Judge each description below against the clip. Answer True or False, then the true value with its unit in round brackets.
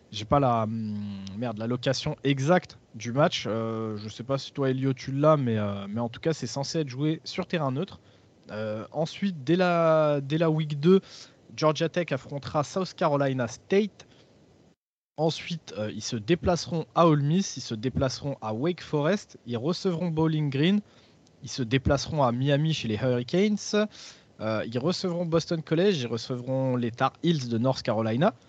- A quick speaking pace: False (175 wpm)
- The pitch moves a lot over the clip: True (5.7 semitones)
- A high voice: False (140 Hz)